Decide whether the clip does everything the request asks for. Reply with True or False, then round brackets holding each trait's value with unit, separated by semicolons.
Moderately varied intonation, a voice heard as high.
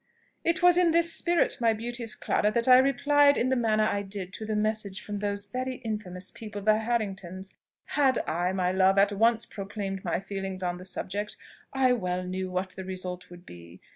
True (4.2 semitones; 205 Hz)